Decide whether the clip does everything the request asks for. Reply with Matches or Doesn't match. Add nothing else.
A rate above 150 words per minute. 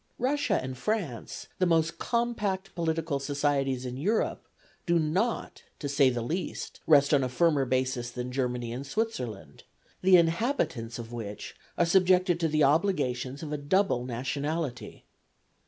Doesn't match